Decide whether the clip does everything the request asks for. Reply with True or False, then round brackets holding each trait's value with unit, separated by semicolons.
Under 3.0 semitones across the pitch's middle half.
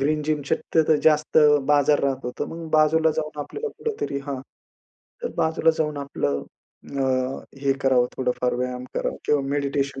True (2.5 semitones)